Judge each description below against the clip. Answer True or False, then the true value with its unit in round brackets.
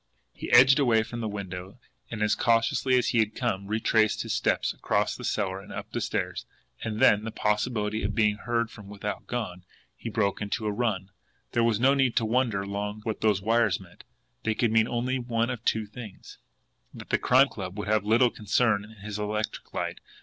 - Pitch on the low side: True (110 Hz)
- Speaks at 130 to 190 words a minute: False (205 wpm)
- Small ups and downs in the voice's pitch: True (2.2 semitones)